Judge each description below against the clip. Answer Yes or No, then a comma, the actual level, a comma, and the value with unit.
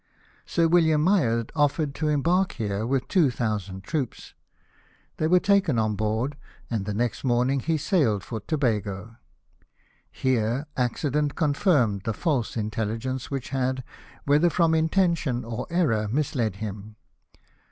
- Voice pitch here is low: Yes, low, 130 Hz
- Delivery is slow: Yes, slow, 130 wpm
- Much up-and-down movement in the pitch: Yes, wide, 5.9 semitones